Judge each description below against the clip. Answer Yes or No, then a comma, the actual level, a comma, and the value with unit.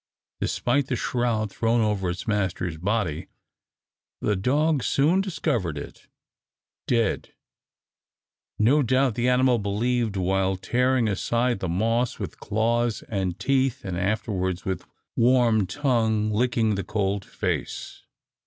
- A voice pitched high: No, low, 110 Hz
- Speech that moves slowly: Yes, slow, 120 wpm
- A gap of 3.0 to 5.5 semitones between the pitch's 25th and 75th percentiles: Yes, average, 4.3 semitones